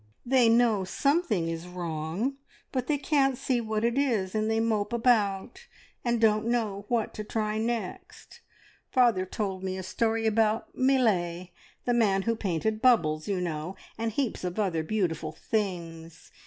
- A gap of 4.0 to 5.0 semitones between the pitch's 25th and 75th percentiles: Yes, average, 4.4 semitones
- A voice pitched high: Yes, high, 215 Hz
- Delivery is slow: No, average, 155 wpm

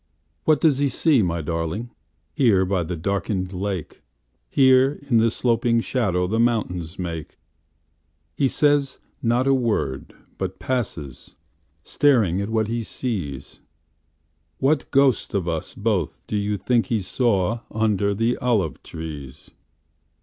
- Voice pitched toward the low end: Yes, low, 100 Hz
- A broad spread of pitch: Yes, wide, 6.5 semitones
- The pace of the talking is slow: Yes, slow, 115 wpm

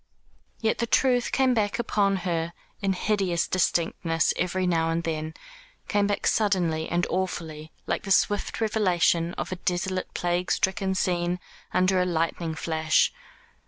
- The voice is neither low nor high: Yes, medium, 180 Hz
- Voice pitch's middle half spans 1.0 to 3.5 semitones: Yes, average, 3.0 semitones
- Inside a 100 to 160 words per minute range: Yes, average, 145 wpm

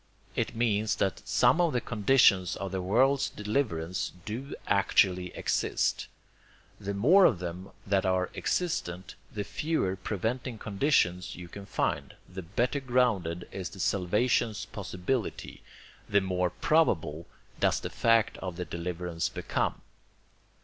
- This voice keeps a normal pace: No, slow, 130 wpm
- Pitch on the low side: Yes, low, 100 Hz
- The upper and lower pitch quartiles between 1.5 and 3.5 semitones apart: No, average, 4.9 semitones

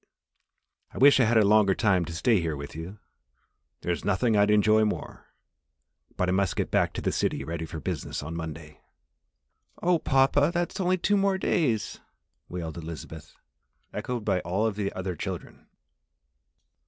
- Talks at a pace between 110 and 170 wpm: Yes, average, 165 wpm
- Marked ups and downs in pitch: Yes, wide, 6.4 semitones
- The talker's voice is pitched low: Yes, low, 100 Hz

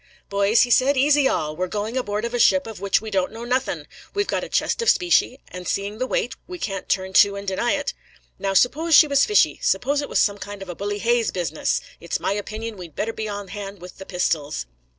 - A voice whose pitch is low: No, high, 210 Hz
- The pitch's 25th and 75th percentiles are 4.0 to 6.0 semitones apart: Yes, average, 4.8 semitones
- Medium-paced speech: No, fast, 240 wpm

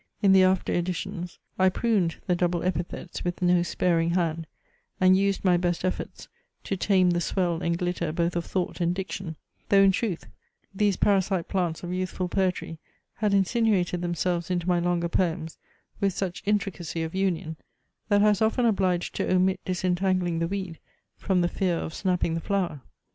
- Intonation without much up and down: Yes, narrow, 1.8 semitones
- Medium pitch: Yes, medium, 180 Hz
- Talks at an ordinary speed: Yes, average, 175 wpm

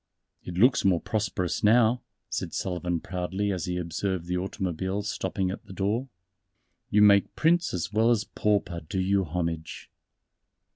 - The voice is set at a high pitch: No, very low, 95 Hz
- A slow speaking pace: No, average, 150 wpm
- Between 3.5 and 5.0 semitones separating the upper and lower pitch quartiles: No, average, 2.8 semitones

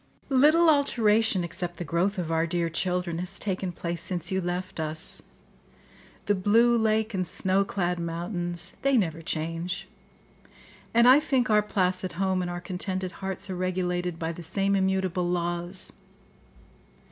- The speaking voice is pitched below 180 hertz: No, medium, 185 Hz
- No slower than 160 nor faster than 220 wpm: No, average, 145 wpm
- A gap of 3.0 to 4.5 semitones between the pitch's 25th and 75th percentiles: No, narrow, 2.5 semitones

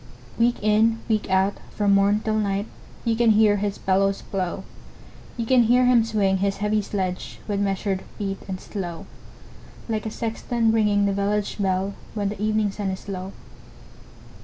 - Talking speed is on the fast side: No, average, 165 wpm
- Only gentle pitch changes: Yes, narrow, 1.8 semitones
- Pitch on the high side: Yes, high, 205 Hz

